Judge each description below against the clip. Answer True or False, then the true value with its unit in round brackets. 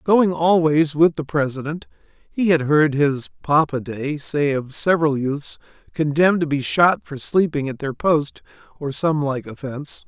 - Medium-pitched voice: True (150 Hz)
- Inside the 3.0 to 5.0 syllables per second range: True (4.4 syllables/s)